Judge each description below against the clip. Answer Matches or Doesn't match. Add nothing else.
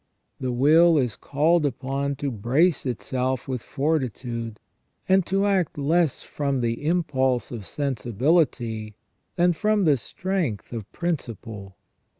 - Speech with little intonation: Doesn't match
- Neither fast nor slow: Doesn't match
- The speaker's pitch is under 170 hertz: Matches